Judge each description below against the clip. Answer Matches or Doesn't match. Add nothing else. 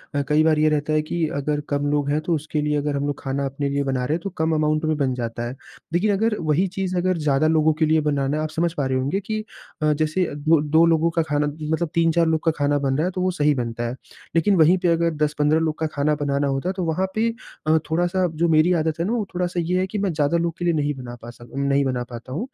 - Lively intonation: Doesn't match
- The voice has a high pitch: Doesn't match